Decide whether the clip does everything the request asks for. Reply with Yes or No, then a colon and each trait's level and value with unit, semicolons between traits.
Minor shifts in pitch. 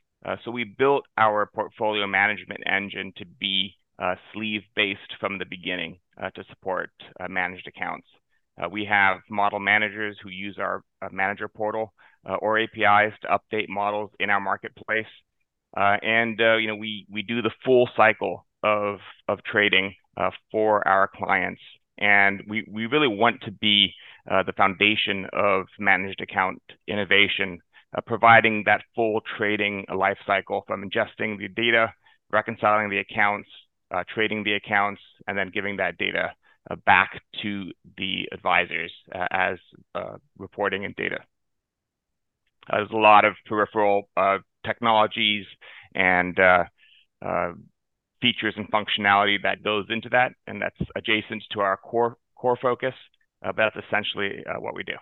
Yes: narrow, 1.8 semitones